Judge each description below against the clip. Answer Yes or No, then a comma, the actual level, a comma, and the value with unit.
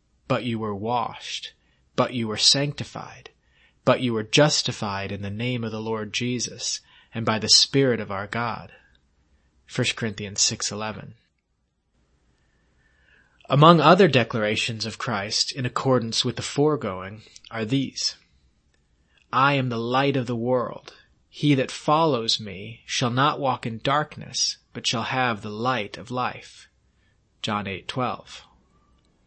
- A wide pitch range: No, average, 4.3 semitones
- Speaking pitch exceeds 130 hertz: No, low, 115 Hz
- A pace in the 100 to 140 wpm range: Yes, slow, 135 wpm